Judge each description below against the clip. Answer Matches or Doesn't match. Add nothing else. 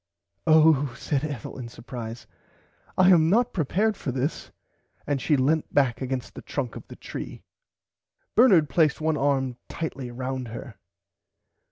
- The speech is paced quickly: Doesn't match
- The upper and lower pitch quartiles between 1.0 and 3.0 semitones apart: Doesn't match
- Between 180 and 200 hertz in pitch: Doesn't match